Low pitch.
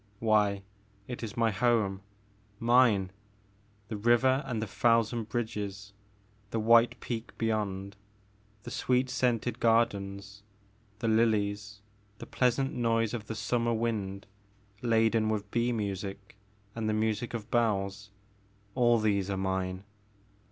Yes: low, 110 Hz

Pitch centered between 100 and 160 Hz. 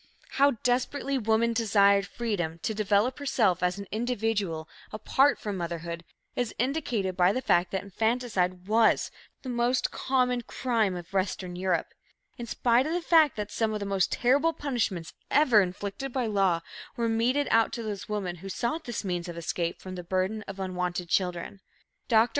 No: high, 210 Hz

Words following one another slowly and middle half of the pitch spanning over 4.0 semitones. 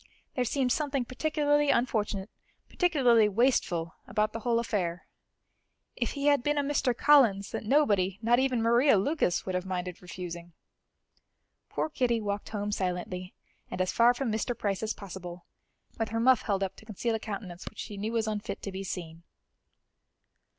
No: average, 170 wpm; average, 4.9 semitones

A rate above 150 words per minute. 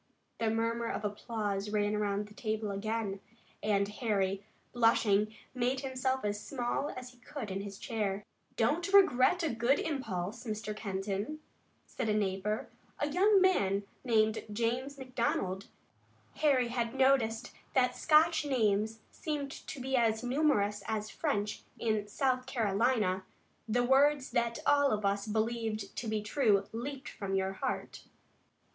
No: average, 140 wpm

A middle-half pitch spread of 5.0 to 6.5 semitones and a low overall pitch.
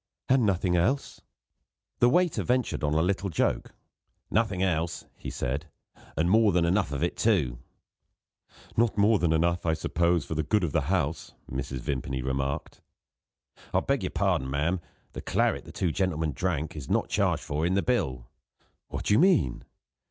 Yes: average, 5.3 semitones; very low, 85 Hz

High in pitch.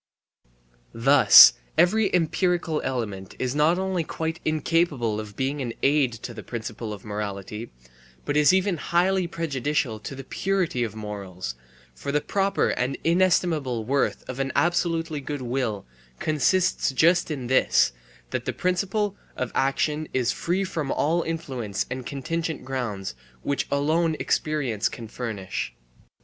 No: medium, 140 Hz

